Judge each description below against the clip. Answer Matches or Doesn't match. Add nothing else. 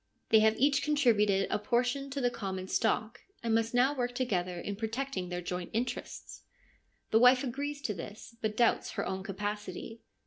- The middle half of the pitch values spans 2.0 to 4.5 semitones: Matches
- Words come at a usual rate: Matches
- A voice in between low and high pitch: Doesn't match